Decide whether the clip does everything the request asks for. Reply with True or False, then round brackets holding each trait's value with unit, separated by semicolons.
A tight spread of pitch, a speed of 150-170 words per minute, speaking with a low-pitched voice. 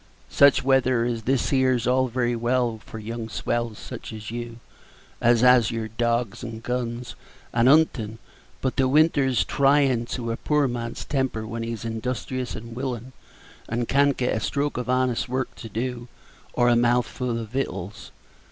True (2.0 semitones; 165 wpm; 120 Hz)